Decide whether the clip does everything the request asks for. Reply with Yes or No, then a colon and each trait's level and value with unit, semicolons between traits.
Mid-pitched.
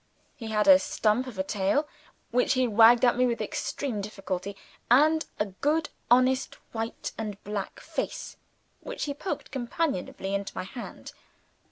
No: high, 235 Hz